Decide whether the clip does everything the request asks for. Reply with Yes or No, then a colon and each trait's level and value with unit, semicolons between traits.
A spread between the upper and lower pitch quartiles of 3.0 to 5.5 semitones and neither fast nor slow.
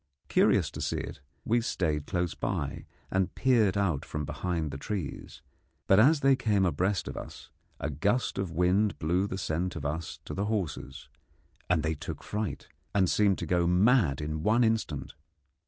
Yes: average, 5.0 semitones; average, 175 wpm